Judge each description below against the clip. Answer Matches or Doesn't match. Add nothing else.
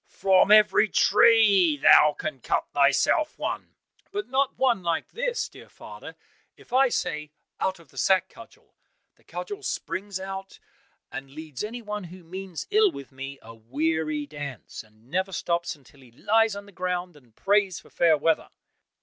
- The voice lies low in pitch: Doesn't match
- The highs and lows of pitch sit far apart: Matches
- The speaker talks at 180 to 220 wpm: Doesn't match